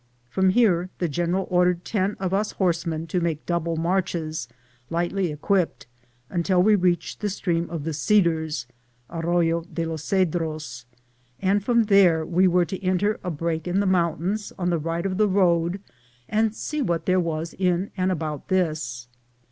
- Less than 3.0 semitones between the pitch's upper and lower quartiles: Yes, narrow, 2.5 semitones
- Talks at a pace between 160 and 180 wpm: Yes, average, 165 wpm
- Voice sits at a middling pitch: Yes, medium, 175 Hz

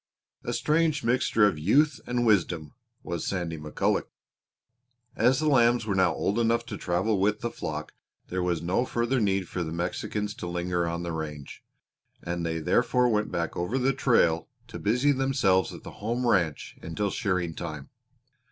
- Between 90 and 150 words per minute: No, average, 170 wpm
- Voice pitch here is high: No, very low, 95 Hz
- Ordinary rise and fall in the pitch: No, wide, 5.8 semitones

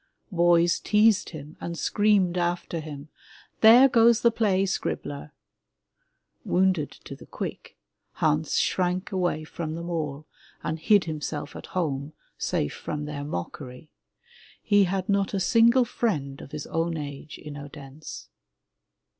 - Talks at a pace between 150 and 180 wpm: No, slow, 135 wpm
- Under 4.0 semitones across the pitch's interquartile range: No, average, 4.7 semitones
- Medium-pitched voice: Yes, medium, 170 Hz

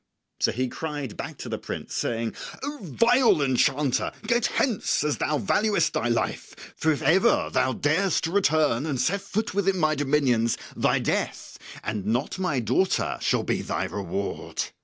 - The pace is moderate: Yes, average, 165 wpm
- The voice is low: No, medium, 150 Hz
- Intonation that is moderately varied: No, wide, 7.5 semitones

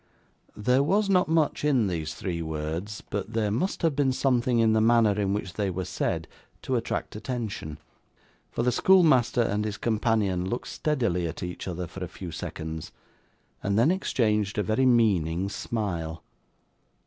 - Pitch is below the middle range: Yes, low, 105 Hz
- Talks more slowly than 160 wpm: No, average, 165 wpm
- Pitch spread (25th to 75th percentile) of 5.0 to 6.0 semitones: Yes, wide, 5.4 semitones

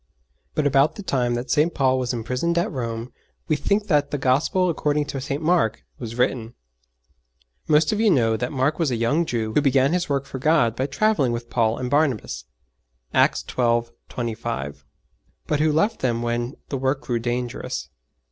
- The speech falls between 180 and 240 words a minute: Yes, average, 185 wpm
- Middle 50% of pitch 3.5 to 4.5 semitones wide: Yes, average, 4.2 semitones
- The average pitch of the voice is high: No, low, 130 Hz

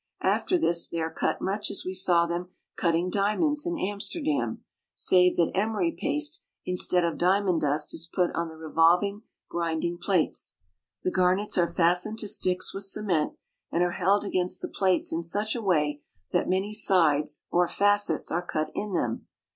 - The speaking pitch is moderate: Yes, medium, 180 Hz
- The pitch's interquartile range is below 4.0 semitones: Yes, average, 3.3 semitones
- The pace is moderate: Yes, average, 175 wpm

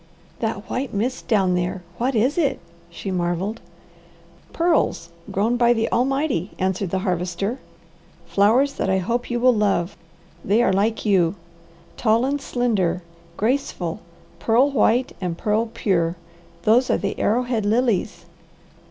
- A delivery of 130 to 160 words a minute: Yes, slow, 135 wpm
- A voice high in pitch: Yes, high, 220 Hz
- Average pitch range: Yes, average, 4.5 semitones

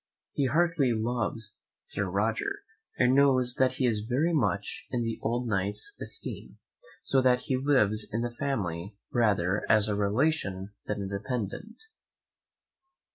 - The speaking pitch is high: No, low, 115 Hz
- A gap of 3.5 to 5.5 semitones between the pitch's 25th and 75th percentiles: Yes, average, 4.2 semitones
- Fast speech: No, average, 140 wpm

